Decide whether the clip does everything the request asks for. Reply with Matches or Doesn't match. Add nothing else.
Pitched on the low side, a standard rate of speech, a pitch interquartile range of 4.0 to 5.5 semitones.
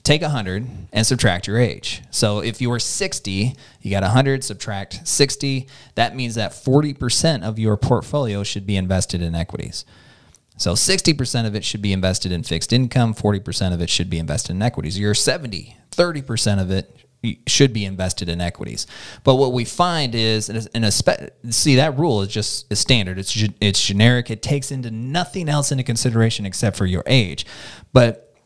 Matches